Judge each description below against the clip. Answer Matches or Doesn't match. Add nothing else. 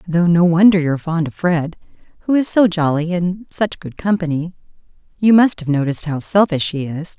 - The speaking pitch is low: Doesn't match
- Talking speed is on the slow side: Doesn't match